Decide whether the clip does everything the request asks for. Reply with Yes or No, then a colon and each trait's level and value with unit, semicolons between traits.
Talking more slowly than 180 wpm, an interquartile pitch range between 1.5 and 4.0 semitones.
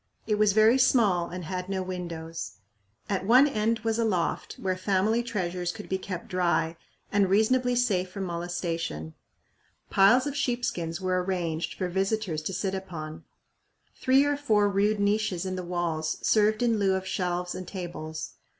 Yes: average, 170 wpm; average, 3.5 semitones